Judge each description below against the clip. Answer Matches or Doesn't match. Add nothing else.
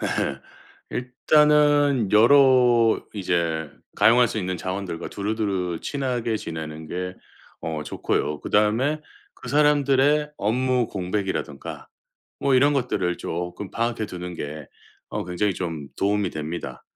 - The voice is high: Doesn't match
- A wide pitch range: Matches